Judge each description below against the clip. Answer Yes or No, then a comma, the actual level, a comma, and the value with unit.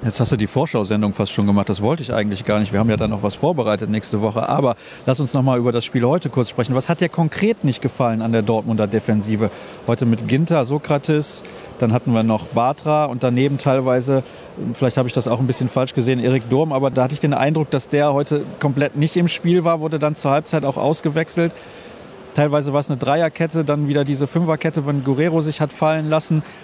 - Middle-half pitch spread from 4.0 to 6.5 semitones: Yes, average, 4.4 semitones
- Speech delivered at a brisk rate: Yes, fast, 230 wpm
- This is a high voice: No, low, 135 Hz